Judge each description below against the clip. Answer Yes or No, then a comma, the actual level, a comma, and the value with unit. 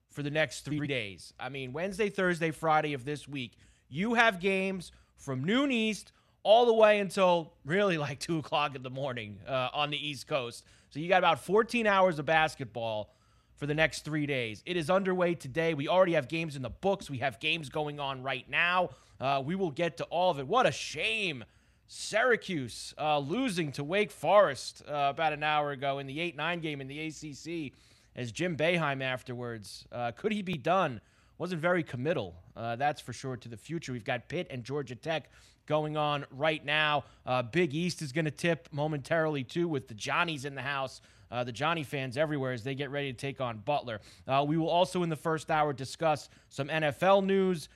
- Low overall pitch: No, medium, 150 Hz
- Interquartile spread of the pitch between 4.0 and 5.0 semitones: Yes, average, 4.6 semitones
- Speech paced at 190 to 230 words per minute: Yes, fast, 205 wpm